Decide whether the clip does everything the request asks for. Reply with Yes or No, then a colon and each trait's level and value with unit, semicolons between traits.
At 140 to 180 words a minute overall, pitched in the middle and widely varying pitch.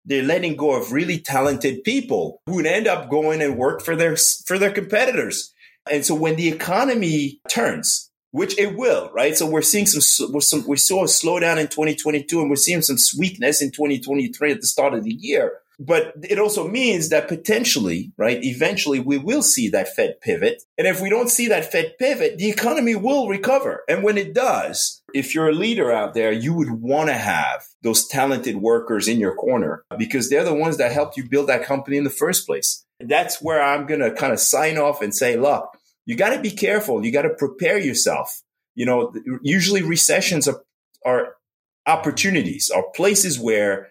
No: fast, 205 wpm; medium, 160 Hz; wide, 8.1 semitones